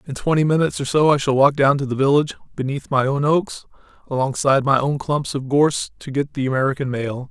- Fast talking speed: Yes, fast, 220 wpm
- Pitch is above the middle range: No, medium, 140 Hz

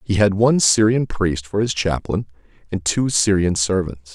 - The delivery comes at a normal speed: Yes, average, 175 wpm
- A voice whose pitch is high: No, low, 100 Hz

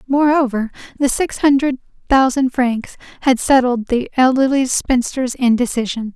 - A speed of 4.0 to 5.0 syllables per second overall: Yes, 4.6 syllables/s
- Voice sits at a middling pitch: No, very high, 255 Hz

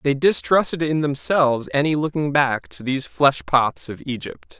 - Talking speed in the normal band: Yes, average, 170 wpm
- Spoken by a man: Yes, male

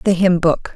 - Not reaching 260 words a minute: Yes, fast, 240 wpm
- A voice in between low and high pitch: Yes, medium, 180 Hz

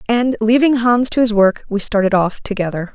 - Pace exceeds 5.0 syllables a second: Yes, 5.3 syllables/s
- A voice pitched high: Yes, high, 220 Hz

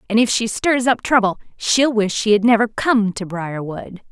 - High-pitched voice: Yes, high, 215 Hz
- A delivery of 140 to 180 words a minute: No, fast, 205 wpm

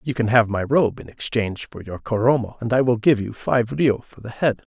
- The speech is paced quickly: Yes, fast, 250 wpm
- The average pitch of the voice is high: No, low, 115 Hz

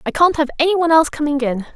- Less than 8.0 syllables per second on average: No, 8.1 syllables/s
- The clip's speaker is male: No, female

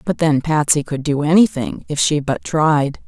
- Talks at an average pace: Yes, average, 195 wpm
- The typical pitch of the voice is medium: Yes, medium, 150 Hz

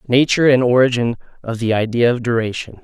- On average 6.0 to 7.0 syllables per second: Yes, 6.1 syllables/s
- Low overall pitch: Yes, low, 120 Hz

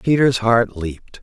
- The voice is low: Yes, low, 115 Hz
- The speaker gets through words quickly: No, average, 145 wpm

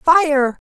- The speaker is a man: No, female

